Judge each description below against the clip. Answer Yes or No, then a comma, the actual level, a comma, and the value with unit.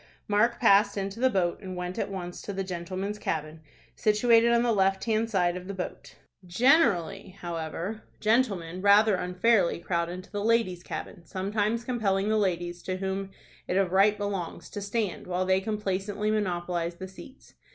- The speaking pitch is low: No, high, 195 Hz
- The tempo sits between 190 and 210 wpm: No, average, 170 wpm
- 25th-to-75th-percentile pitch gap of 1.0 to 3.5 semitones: Yes, average, 2.9 semitones